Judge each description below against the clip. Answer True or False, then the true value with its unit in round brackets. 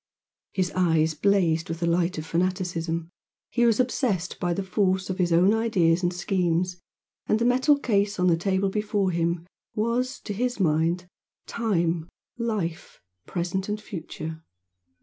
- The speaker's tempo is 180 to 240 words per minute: False (150 wpm)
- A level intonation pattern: False (3.7 semitones)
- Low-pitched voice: False (185 Hz)